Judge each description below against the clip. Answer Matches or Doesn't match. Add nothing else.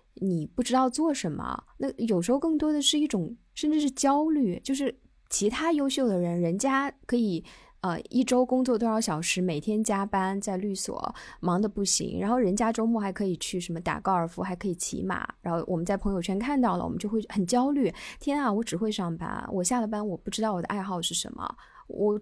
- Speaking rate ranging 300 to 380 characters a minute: Matches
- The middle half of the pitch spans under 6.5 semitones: Matches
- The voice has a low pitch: Doesn't match